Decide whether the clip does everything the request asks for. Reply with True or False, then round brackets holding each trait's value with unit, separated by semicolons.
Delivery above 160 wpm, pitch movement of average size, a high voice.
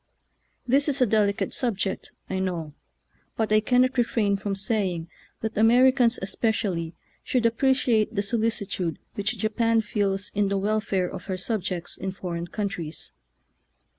False (155 wpm; 3.2 semitones; 210 Hz)